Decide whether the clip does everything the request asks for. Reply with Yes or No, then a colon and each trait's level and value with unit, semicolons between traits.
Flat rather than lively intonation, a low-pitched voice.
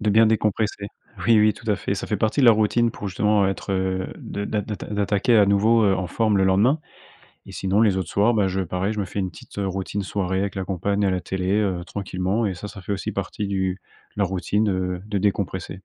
Yes: narrow, 2.0 semitones; low, 100 Hz